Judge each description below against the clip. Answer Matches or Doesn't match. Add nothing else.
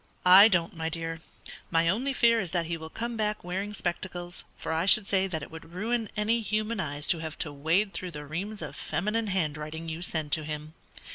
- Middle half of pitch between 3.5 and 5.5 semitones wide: Matches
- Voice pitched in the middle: Matches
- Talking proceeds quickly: Matches